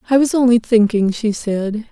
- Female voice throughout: Yes, female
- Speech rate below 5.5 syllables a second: Yes, 4.8 syllables/s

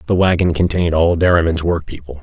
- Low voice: Yes, very low, 85 Hz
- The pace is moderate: Yes, average, 160 wpm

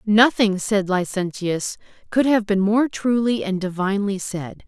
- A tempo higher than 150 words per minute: No, average, 140 wpm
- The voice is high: Yes, high, 205 Hz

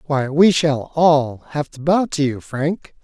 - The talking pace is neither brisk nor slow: Yes, average, 195 wpm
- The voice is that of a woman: No, male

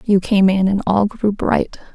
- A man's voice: No, female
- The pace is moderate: No, fast, 215 wpm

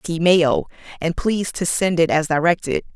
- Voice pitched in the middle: Yes, medium, 170 Hz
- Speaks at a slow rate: No, average, 185 wpm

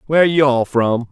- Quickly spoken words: Yes, fast, 215 wpm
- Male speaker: Yes, male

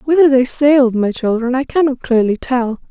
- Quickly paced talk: No, average, 185 wpm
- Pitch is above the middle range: Yes, very high, 260 Hz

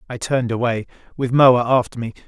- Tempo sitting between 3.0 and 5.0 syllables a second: No, 6.0 syllables/s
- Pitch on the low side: Yes, low, 120 Hz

